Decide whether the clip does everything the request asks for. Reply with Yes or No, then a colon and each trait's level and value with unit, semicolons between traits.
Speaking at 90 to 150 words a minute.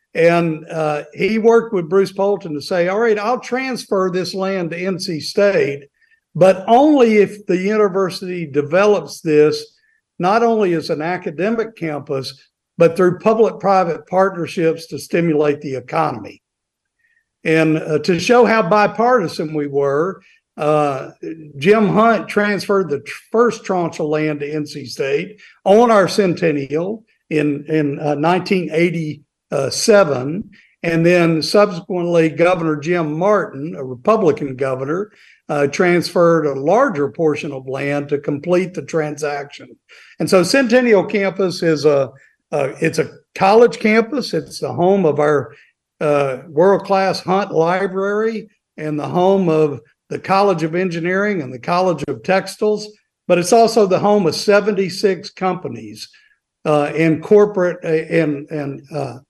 Yes: average, 140 wpm